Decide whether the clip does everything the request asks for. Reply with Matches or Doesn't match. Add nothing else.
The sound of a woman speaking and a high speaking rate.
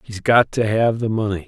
Doesn't match